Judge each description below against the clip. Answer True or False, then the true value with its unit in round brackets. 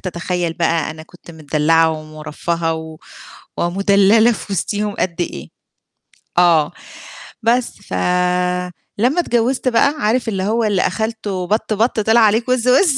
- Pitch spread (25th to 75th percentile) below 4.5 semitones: False (5.2 semitones)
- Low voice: False (190 Hz)